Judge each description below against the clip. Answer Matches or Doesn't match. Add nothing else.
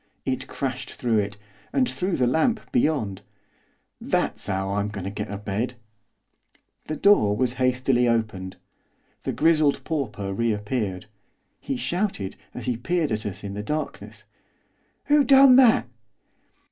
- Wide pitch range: Matches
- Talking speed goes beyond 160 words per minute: Doesn't match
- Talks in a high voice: Doesn't match